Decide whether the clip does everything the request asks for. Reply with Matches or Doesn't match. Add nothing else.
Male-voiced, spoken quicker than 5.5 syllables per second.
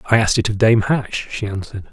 Matches